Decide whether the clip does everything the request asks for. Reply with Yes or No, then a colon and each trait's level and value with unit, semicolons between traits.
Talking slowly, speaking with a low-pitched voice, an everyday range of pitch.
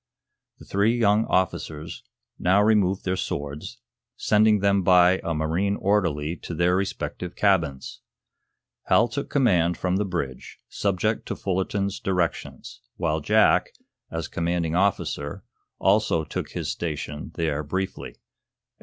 Yes: slow, 125 wpm; very low, 90 Hz; average, 3.5 semitones